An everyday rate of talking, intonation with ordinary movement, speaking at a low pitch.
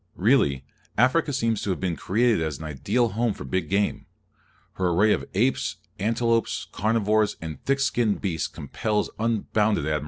Yes: average, 160 wpm; average, 4.6 semitones; low, 105 Hz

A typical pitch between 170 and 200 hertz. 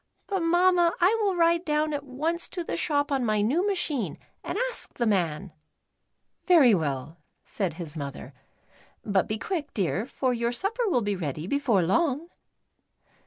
No: very high, 270 Hz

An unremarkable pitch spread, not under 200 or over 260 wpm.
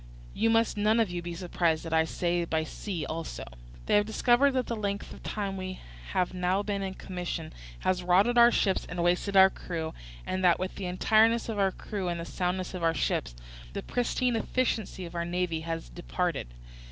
Yes: average, 3.2 semitones; fast, 205 wpm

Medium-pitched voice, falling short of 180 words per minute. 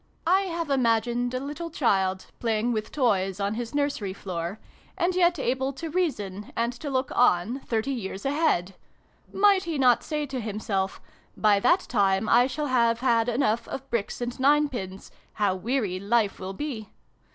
No: high, 240 Hz; average, 170 wpm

